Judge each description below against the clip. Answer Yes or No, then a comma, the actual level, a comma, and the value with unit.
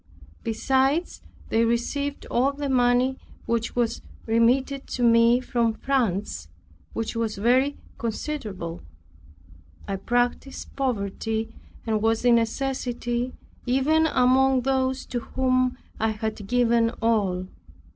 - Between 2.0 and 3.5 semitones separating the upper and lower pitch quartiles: Yes, average, 2.7 semitones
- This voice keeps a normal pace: No, slow, 110 wpm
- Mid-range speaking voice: No, high, 240 Hz